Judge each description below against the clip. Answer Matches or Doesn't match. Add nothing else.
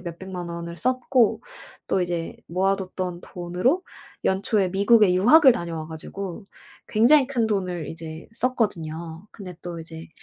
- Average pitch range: Matches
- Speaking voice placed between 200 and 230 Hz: Doesn't match